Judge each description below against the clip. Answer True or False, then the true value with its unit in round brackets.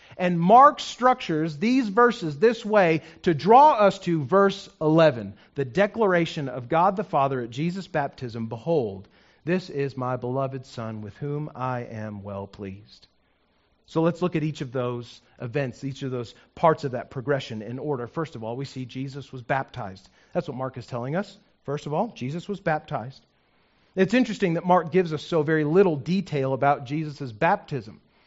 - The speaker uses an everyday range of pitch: False (5.9 semitones)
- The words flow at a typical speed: True (180 wpm)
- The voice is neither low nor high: True (150 Hz)